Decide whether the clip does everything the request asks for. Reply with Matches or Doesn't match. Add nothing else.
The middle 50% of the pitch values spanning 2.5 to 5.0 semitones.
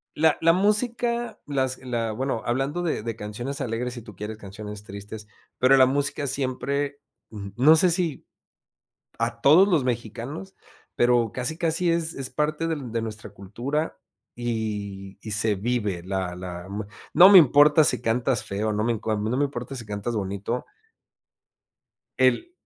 Doesn't match